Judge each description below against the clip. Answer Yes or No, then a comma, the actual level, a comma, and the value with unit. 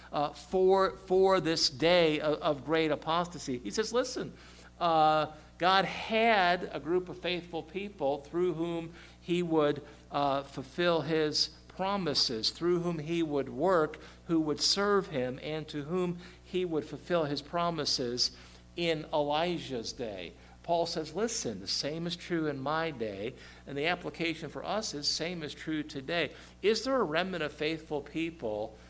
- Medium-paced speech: Yes, average, 155 wpm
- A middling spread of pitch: Yes, average, 3.1 semitones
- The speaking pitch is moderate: Yes, medium, 160 Hz